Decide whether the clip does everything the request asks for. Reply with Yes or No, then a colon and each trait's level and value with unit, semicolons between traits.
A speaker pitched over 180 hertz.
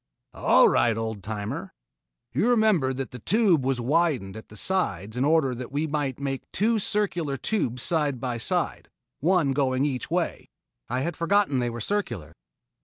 No: low, 135 Hz